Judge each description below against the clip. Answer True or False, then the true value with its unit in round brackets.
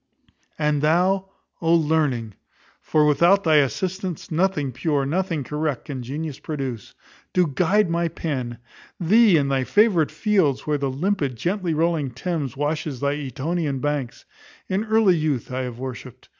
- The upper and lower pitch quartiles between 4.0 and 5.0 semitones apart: True (4.4 semitones)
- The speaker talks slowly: False (150 wpm)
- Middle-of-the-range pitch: True (155 Hz)